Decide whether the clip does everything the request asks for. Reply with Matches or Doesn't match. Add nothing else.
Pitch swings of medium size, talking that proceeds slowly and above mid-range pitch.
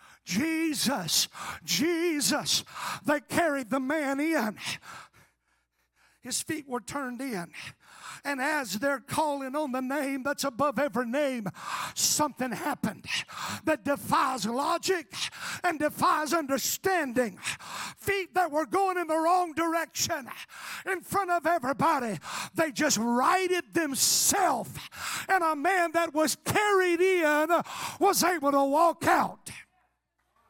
Matches